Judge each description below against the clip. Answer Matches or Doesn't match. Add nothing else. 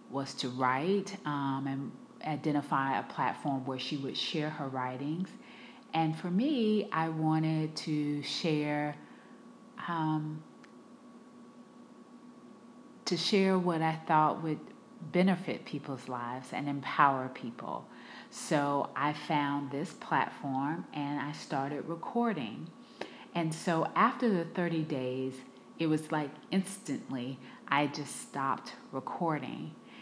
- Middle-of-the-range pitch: Matches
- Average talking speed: Doesn't match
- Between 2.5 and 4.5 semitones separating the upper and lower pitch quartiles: Doesn't match